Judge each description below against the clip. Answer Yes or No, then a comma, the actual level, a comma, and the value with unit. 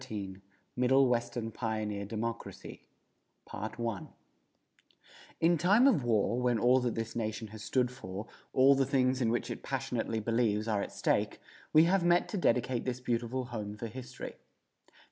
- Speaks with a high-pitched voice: No, low, 120 Hz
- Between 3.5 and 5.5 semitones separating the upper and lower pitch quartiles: No, average, 2.9 semitones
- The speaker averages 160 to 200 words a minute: No, average, 150 wpm